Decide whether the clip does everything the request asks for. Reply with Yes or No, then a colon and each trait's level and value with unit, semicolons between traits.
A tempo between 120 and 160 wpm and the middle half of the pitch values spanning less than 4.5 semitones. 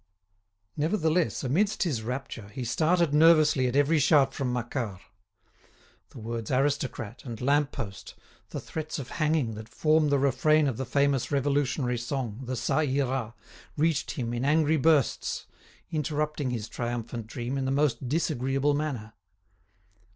Yes: average, 145 wpm; average, 4.0 semitones